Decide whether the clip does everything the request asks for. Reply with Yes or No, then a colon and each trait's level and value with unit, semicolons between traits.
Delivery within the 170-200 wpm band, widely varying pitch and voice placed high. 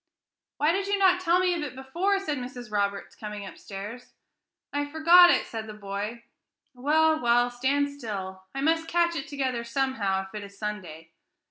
Yes: average, 175 wpm; wide, 7.1 semitones; very high, 255 Hz